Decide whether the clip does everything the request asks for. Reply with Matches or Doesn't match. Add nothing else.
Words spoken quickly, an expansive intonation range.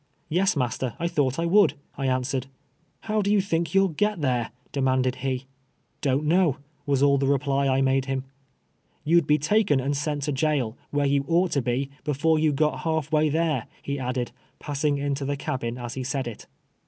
Doesn't match